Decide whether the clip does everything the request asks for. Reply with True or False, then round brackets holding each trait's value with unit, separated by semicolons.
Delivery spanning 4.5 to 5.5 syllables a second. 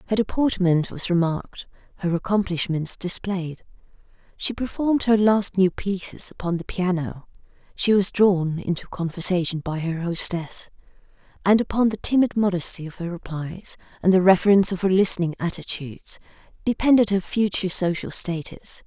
True (5.2 syllables/s)